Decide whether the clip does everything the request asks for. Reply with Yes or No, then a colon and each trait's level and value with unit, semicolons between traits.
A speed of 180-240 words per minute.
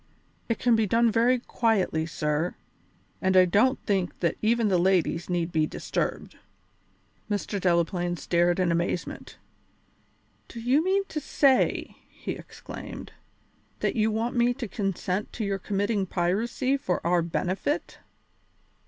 No: slow, 135 wpm